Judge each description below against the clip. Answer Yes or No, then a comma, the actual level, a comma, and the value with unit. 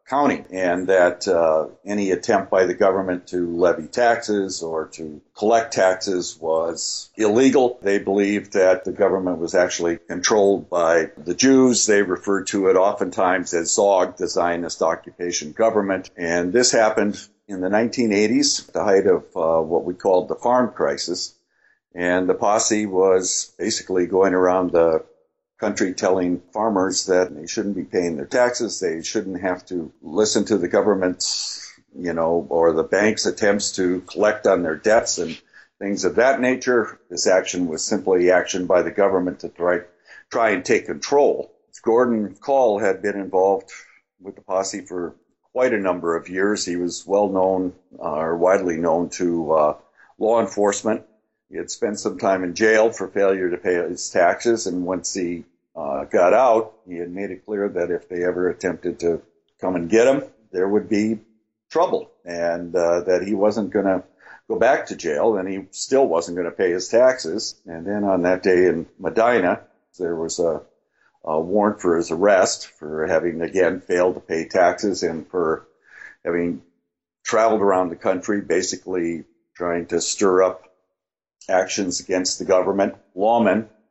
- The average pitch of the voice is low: Yes, very low, 95 Hz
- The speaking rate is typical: Yes, average, 170 wpm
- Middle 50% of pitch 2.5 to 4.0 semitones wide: Yes, average, 3.1 semitones